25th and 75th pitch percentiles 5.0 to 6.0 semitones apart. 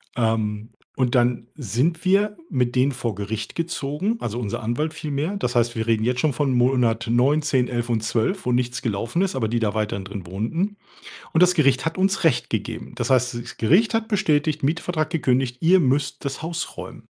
Yes: wide, 5.4 semitones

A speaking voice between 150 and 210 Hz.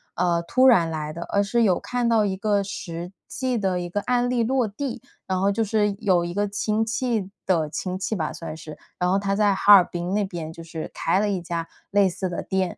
Yes: high, 195 Hz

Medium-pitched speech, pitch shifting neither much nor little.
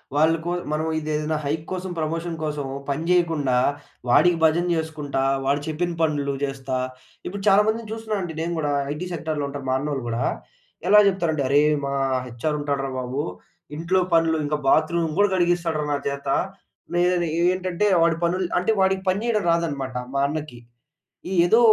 Yes: medium, 160 Hz; average, 3.4 semitones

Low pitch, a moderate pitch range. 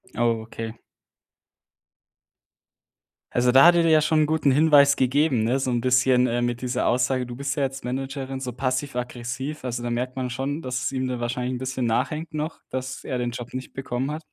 No: low, 130 Hz; narrow, 2.0 semitones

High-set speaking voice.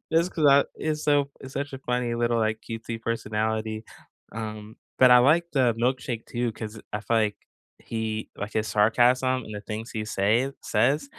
No: low, 115 Hz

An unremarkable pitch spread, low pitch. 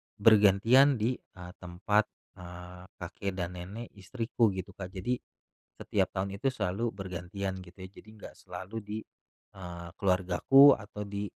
Yes: average, 3.1 semitones; low, 100 Hz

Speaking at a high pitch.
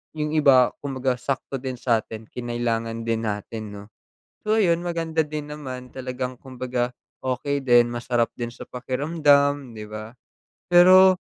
No: low, 130 Hz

